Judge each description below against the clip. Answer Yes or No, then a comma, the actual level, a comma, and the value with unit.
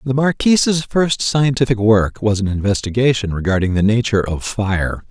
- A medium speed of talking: Yes, average, 155 wpm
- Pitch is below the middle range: Yes, low, 115 Hz